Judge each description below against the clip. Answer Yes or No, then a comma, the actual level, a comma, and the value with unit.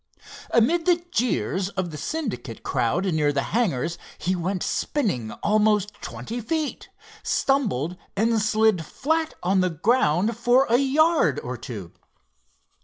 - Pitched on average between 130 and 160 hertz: No, high, 210 Hz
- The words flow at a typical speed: No, slow, 130 wpm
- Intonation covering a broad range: Yes, wide, 7.1 semitones